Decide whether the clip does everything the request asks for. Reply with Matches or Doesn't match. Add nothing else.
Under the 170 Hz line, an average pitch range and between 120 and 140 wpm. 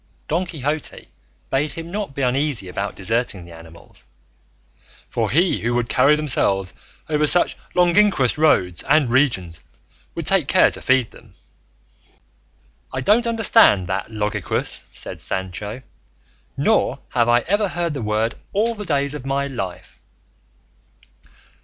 Doesn't match